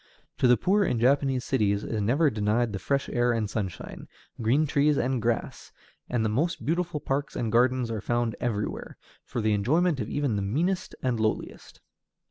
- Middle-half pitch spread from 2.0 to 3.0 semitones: No, average, 4.4 semitones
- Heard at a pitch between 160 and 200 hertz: No, low, 120 Hz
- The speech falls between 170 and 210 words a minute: Yes, average, 175 wpm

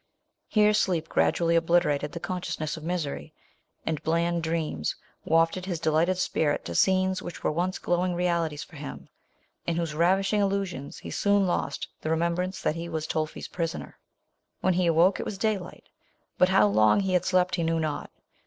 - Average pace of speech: Yes, average, 175 wpm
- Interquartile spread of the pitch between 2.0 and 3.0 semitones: Yes, narrow, 2.5 semitones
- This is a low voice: No, medium, 170 Hz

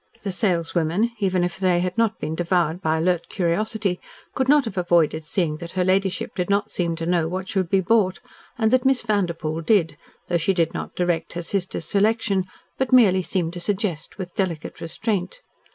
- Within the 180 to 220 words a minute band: Yes, average, 190 wpm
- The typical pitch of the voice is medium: Yes, medium, 180 Hz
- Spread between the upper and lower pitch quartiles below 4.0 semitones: Yes, average, 3.2 semitones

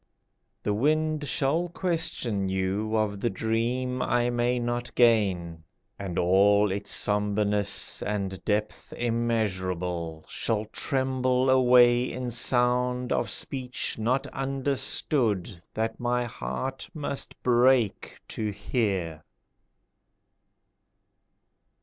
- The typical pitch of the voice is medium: No, low, 120 Hz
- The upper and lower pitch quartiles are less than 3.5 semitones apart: No, average, 3.8 semitones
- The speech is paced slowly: Yes, slow, 95 wpm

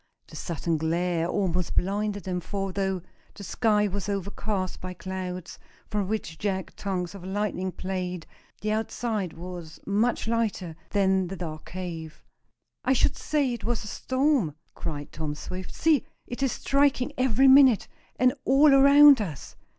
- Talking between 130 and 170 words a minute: Yes, average, 150 wpm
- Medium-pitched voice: No, high, 195 Hz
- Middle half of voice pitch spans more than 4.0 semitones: Yes, average, 4.4 semitones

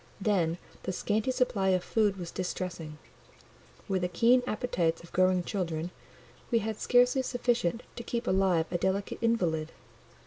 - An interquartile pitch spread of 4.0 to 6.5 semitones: Yes, average, 4.7 semitones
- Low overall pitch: No, high, 190 Hz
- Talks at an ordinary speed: Yes, average, 145 wpm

